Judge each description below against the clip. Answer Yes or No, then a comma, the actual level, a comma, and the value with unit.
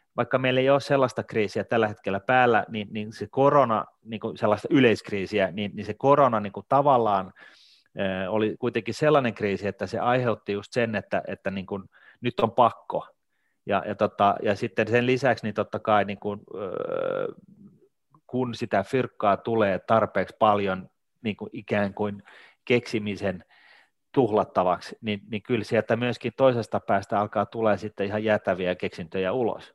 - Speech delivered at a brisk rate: Yes, fast, 160 wpm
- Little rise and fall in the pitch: No, average, 3.1 semitones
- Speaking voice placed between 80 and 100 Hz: No, low, 110 Hz